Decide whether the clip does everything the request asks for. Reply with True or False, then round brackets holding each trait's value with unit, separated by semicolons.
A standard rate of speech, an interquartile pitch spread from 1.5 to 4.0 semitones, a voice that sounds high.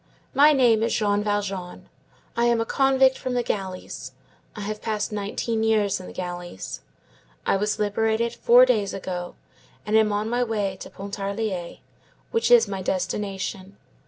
True (160 wpm; 2.9 semitones; 210 Hz)